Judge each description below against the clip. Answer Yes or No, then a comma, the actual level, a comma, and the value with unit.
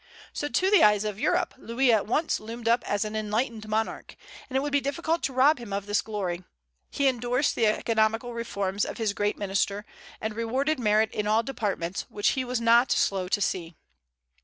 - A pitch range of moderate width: Yes, average, 3.6 semitones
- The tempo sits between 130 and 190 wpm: No, average, 200 wpm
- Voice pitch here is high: Yes, high, 225 Hz